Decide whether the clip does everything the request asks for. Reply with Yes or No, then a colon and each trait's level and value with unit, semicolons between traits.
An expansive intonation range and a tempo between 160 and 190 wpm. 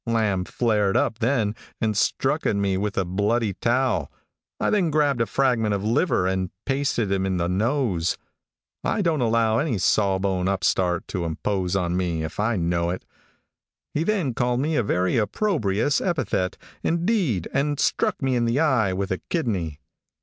Yes: wide, 5.9 semitones; average, 170 wpm